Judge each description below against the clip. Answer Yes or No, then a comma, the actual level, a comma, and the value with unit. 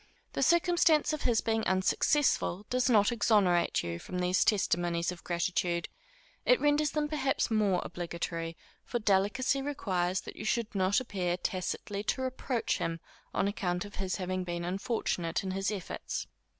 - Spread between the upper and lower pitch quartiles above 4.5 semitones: Yes, wide, 5.6 semitones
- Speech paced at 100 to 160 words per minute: Yes, average, 155 wpm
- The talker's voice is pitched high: Yes, high, 195 Hz